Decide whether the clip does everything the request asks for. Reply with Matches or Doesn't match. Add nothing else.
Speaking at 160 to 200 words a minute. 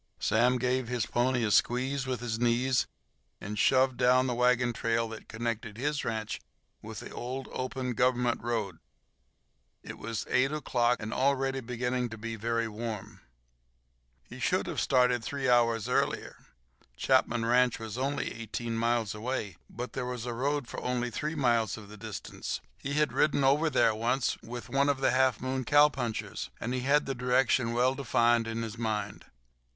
Matches